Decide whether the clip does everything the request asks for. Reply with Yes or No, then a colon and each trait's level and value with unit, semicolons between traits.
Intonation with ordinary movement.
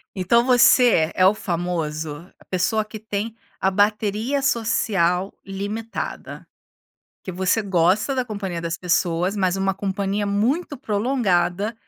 Yes: average, 3.6 semitones